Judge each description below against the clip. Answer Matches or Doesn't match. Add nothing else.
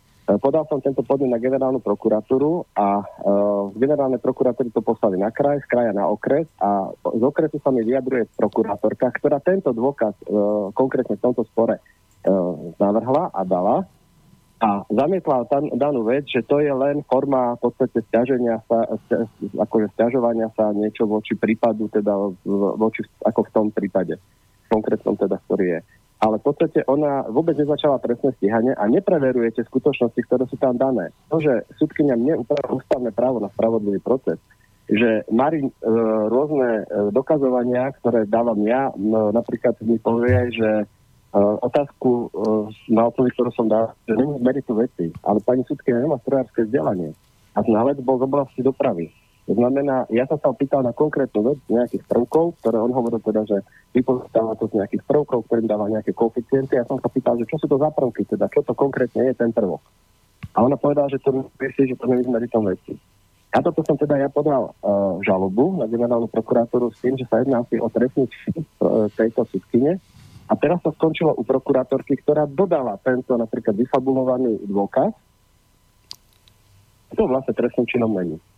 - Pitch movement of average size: Matches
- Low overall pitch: Matches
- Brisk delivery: Matches